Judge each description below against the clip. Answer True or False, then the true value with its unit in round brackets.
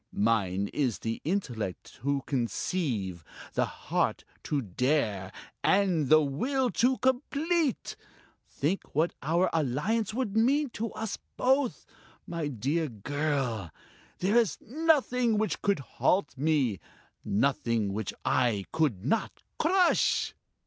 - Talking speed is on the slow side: True (115 wpm)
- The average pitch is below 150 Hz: False (155 Hz)